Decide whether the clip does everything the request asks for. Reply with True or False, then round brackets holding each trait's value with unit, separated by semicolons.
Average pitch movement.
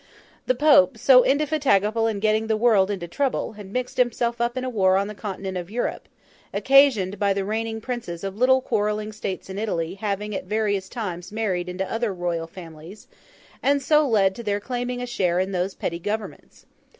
True (4.1 semitones)